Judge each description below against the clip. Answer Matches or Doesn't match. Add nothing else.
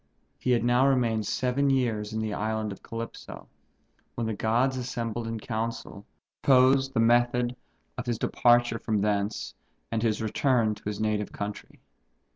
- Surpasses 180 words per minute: Doesn't match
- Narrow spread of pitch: Matches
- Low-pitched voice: Matches